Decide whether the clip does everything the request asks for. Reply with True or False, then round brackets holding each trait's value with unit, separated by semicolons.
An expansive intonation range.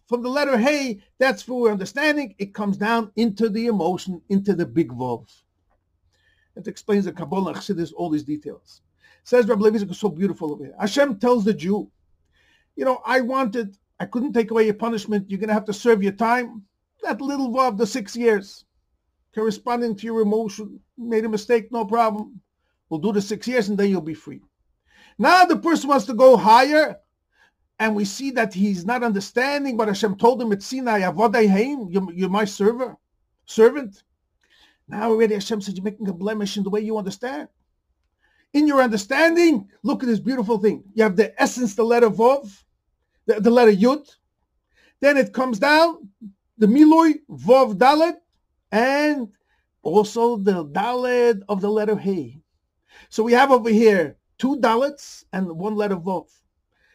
False (3.8 semitones)